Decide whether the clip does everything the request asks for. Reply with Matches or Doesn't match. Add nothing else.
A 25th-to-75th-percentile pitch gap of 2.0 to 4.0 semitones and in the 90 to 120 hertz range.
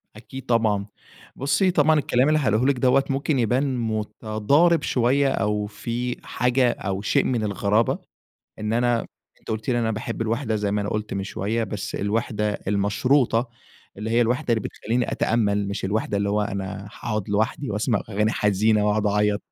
Matches